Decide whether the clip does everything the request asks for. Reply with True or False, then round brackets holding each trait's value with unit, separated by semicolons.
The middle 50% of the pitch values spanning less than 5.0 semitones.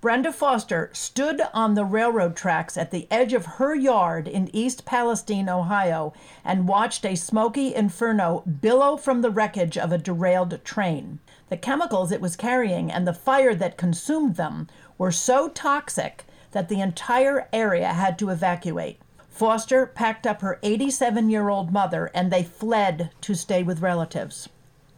False (5.3 semitones)